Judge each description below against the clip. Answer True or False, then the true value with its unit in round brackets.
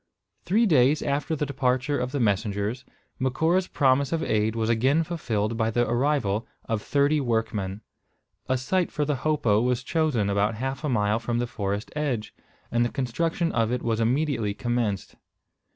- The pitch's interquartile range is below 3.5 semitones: False (4.5 semitones)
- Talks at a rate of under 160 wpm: False (170 wpm)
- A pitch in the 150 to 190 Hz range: False (125 Hz)